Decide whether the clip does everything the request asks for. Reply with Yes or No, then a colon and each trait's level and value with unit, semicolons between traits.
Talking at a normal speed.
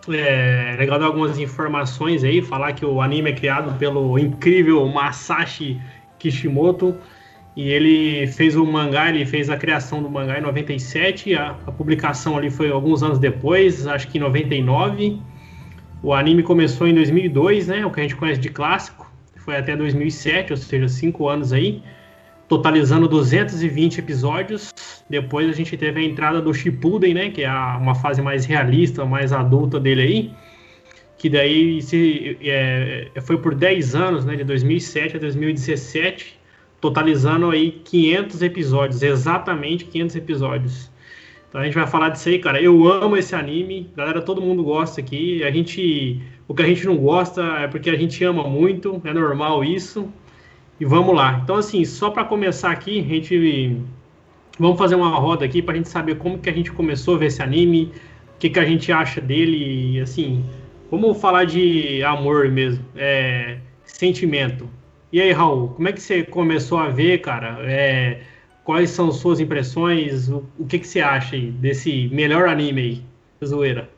Yes: average, 170 wpm